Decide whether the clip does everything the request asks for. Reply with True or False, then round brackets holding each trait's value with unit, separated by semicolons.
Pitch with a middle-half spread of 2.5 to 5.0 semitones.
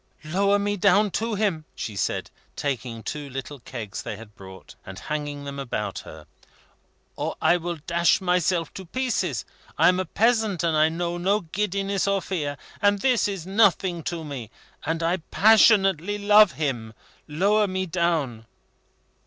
False (5.6 semitones)